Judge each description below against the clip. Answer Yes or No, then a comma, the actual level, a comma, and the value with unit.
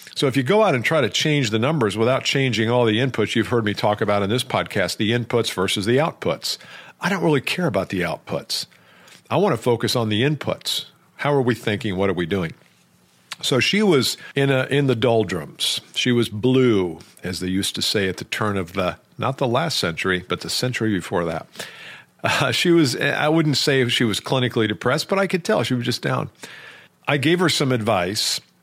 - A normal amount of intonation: Yes, average, 4.6 semitones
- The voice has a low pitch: Yes, low, 120 Hz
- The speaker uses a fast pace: Yes, fast, 220 wpm